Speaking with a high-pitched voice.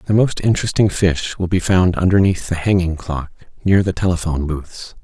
No: very low, 90 Hz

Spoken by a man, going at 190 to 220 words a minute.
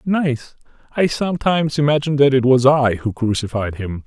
No: male; average, 160 wpm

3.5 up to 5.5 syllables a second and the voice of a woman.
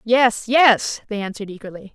Yes: 5.1 syllables/s; female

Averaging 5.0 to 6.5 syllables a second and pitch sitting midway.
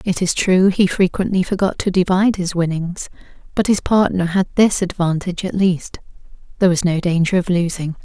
Yes: 5.5 syllables/s; medium, 180 Hz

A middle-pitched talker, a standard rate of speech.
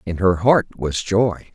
No: low, 100 Hz; average, 195 wpm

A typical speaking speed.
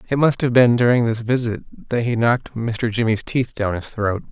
No: fast, 220 wpm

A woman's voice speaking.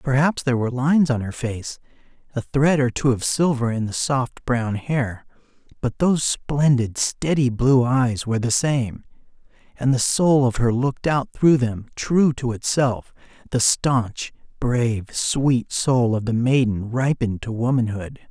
No: male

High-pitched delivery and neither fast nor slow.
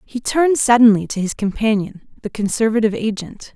Yes: high, 220 Hz; average, 150 wpm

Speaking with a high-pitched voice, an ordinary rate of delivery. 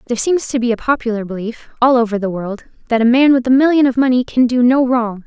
No: high, 240 Hz; fast, 260 wpm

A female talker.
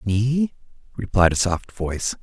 No: male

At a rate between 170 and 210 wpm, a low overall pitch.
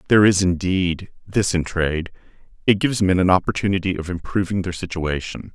No: average, 150 wpm; very low, 90 Hz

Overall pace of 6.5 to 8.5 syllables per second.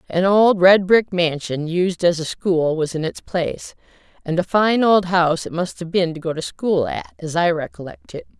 No: 4.8 syllables/s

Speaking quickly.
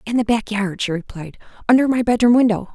Yes: fast, 220 wpm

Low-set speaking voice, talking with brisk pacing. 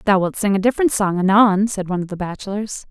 No: high, 200 Hz; fast, 250 wpm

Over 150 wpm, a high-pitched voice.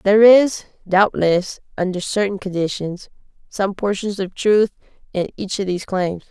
No: average, 145 wpm; high, 195 Hz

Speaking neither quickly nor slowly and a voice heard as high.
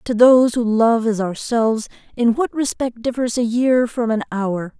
Yes: average, 190 wpm; high, 235 Hz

